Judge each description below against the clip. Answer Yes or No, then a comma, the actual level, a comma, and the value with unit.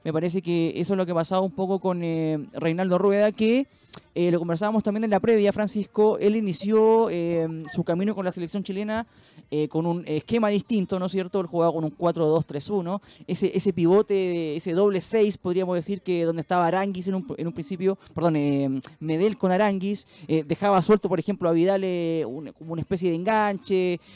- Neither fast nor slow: No, fast, 200 wpm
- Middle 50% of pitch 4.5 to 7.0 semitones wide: No, average, 3.3 semitones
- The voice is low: No, medium, 185 Hz